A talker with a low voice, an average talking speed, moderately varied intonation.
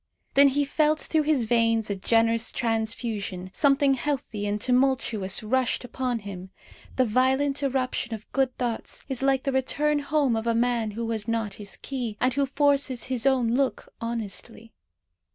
No: high, 245 Hz; average, 165 wpm; average, 3.3 semitones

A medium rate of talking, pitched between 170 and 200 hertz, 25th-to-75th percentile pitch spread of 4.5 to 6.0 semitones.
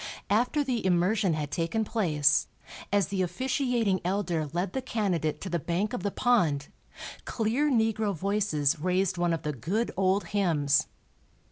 Yes: average, 150 wpm; high, 190 Hz; average, 4.9 semitones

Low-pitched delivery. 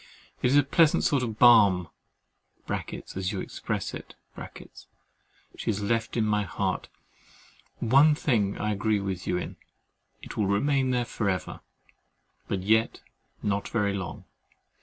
Yes: low, 105 Hz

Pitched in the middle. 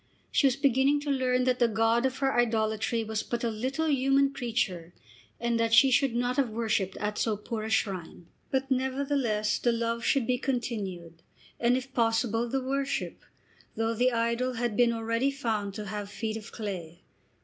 No: high, 235 Hz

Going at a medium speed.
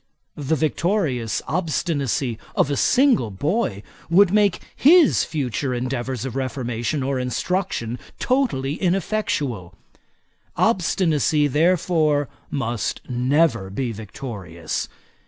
No: slow, 95 wpm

